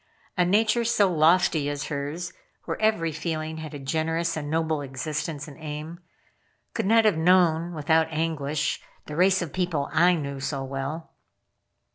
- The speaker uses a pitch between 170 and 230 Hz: No, medium, 160 Hz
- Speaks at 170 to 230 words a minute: No, average, 155 wpm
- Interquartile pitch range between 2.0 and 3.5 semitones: Yes, average, 2.9 semitones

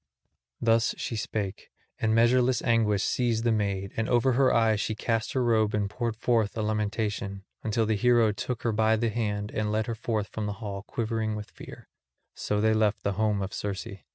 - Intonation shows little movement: Yes, narrow, 1.8 semitones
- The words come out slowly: No, average, 200 wpm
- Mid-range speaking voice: No, low, 110 Hz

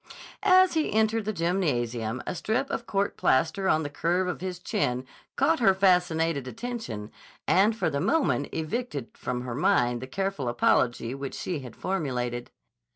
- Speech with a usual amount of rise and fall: No, wide, 8.0 semitones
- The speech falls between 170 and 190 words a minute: No, average, 160 wpm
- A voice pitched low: No, medium, 165 Hz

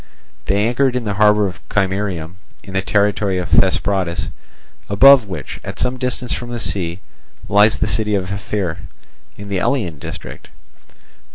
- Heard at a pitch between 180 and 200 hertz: No, low, 100 Hz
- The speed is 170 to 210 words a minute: No, average, 155 wpm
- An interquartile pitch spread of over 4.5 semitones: No, narrow, 2.5 semitones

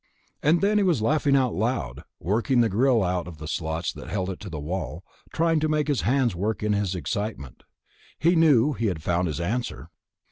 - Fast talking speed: Yes, fast, 210 wpm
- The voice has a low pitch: Yes, low, 110 Hz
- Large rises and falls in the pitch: Yes, wide, 7.8 semitones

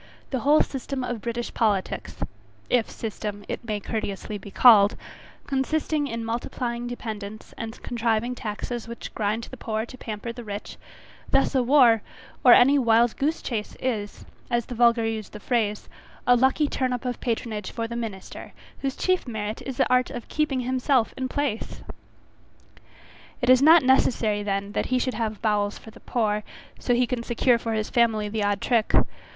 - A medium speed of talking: Yes, average, 175 wpm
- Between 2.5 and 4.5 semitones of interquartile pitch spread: Yes, average, 2.8 semitones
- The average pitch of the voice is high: Yes, high, 235 Hz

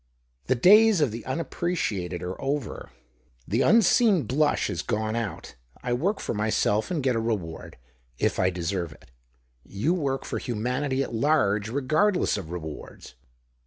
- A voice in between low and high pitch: No, low, 125 Hz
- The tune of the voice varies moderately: No, wide, 7.0 semitones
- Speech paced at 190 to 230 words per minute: No, average, 155 wpm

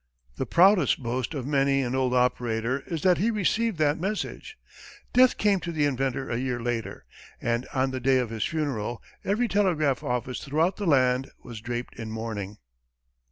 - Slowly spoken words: No, average, 175 wpm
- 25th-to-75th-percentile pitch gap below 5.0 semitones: No, wide, 5.6 semitones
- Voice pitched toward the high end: No, low, 135 Hz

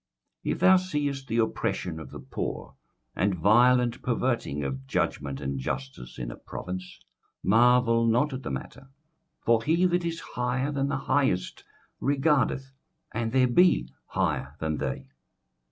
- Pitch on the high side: No, low, 120 Hz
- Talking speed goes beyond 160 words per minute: No, average, 150 wpm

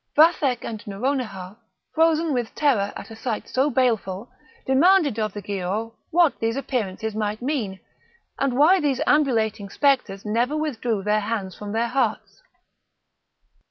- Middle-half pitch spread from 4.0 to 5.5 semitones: Yes, average, 5.0 semitones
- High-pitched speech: Yes, high, 235 Hz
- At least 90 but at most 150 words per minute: Yes, average, 140 wpm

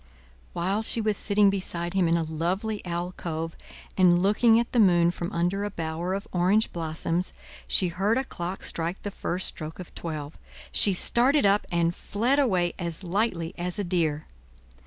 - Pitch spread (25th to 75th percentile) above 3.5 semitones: No, average, 3.1 semitones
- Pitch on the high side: No, medium, 180 Hz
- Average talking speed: Yes, average, 175 wpm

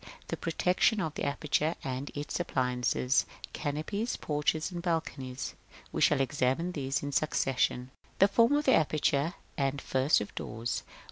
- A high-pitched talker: No, medium, 145 Hz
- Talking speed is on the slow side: No, average, 165 wpm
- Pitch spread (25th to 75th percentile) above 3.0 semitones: Yes, average, 4.1 semitones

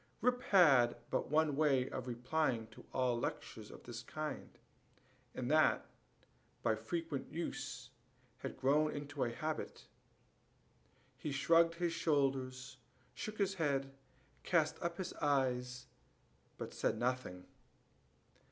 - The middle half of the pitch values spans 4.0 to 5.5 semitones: Yes, average, 4.3 semitones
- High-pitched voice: No, medium, 140 Hz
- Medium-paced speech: No, slow, 120 wpm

